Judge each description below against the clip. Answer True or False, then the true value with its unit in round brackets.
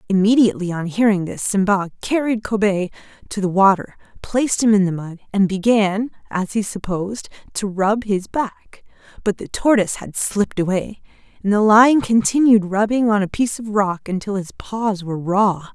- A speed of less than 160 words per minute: False (170 wpm)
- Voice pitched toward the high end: True (205 Hz)